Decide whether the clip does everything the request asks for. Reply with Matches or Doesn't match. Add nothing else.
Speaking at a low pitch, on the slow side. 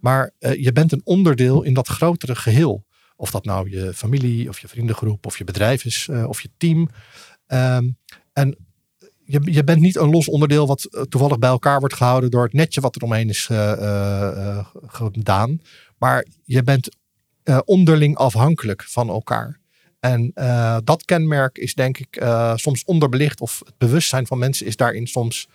Doesn't match